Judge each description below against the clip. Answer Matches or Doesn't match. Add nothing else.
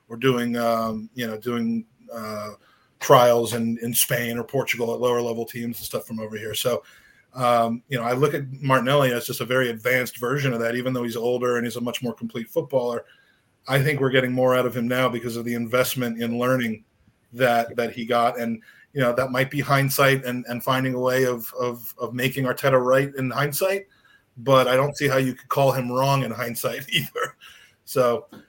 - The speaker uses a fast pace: Matches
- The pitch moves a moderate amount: Doesn't match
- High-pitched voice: Doesn't match